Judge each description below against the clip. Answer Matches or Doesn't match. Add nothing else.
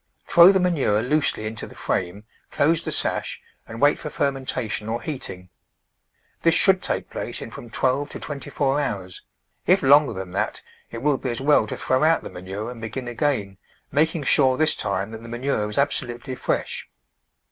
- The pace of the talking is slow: Doesn't match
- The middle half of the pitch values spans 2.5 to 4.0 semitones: Doesn't match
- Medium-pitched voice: Doesn't match